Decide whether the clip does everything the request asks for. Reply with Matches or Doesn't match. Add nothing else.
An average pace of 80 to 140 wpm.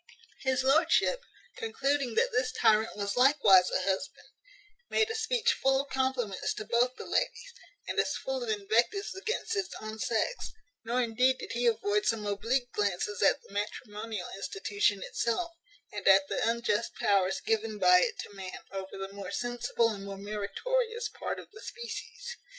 Doesn't match